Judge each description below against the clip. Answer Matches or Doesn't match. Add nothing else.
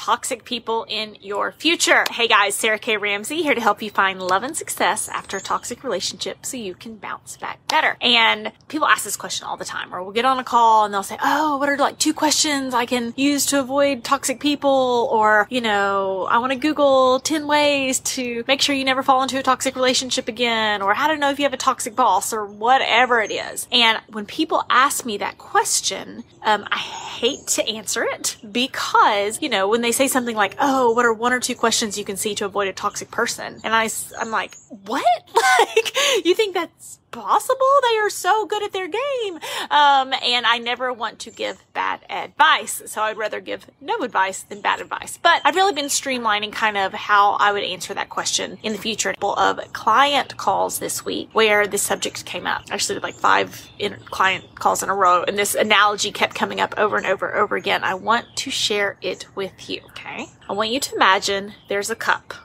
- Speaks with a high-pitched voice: Matches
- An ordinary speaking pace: Doesn't match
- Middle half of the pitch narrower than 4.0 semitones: Doesn't match